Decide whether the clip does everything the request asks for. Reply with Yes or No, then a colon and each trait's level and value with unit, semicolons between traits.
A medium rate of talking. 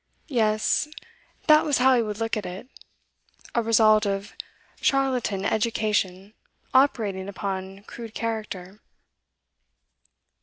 No: slow, 105 wpm